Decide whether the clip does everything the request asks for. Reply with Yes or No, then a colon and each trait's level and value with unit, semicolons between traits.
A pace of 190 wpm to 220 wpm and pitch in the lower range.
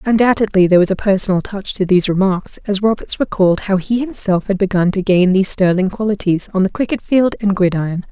No: fast, 205 wpm; high, 195 Hz